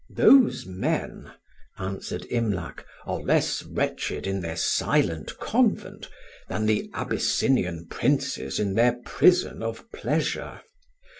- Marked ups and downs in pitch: No, average, 4.4 semitones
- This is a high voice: No, low, 100 Hz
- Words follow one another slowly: Yes, slow, 105 wpm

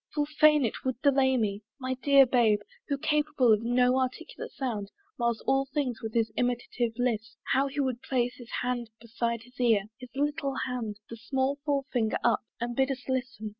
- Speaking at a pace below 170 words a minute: No, average, 185 wpm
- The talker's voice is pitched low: No, very high, 250 Hz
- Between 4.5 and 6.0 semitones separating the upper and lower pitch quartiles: No, average, 2.7 semitones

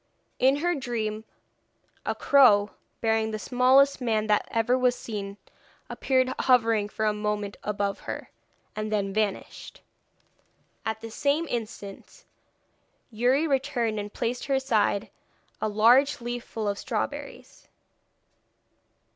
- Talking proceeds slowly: Yes, slow, 125 wpm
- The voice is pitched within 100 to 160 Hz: No, high, 225 Hz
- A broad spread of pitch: No, average, 3.5 semitones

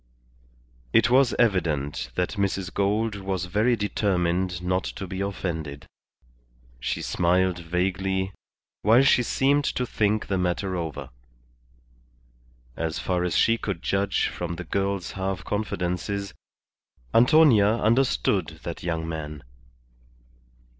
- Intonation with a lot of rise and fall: No, average, 3.1 semitones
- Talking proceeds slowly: Yes, slow, 115 wpm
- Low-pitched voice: Yes, very low, 95 Hz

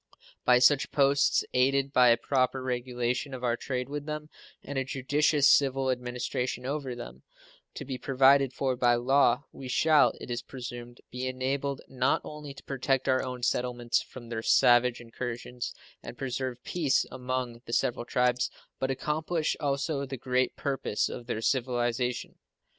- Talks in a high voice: No, low, 130 Hz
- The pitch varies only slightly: Yes, narrow, 2.0 semitones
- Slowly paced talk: No, average, 160 wpm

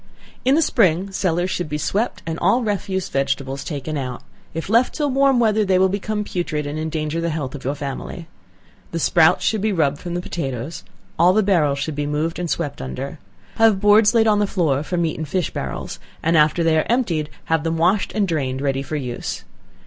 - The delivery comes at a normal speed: No, fast, 210 wpm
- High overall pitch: No, medium, 165 Hz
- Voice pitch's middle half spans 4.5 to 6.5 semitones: Yes, average, 5.1 semitones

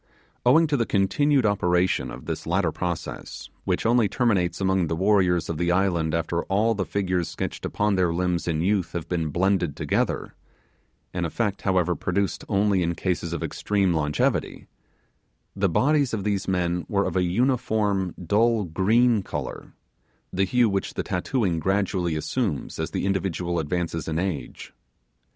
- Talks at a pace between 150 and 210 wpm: Yes, average, 160 wpm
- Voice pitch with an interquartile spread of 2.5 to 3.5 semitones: Yes, average, 3.1 semitones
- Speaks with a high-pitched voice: No, very low, 95 Hz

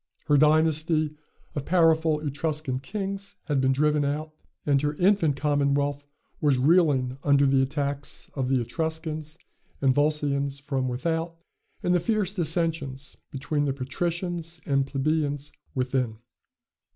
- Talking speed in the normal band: No, slow, 125 wpm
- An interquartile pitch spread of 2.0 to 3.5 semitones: Yes, average, 2.7 semitones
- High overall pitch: No, medium, 150 Hz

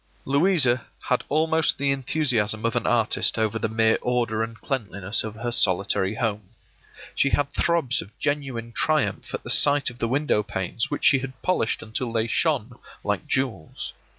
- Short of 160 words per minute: No, average, 170 wpm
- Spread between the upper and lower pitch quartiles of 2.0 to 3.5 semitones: No, average, 4.2 semitones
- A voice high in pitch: No, low, 120 Hz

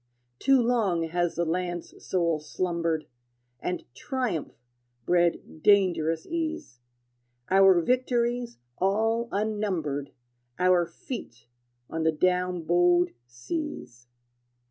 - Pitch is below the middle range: No, medium, 180 Hz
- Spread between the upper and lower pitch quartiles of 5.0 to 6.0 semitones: Yes, average, 5.3 semitones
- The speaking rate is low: Yes, slow, 95 wpm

